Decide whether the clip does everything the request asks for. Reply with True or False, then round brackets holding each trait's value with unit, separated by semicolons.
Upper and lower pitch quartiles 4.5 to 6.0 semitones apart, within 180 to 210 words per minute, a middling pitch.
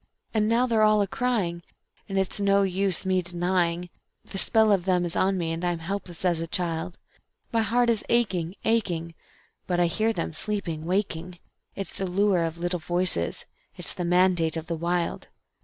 False (2.8 semitones; 185 wpm; 180 Hz)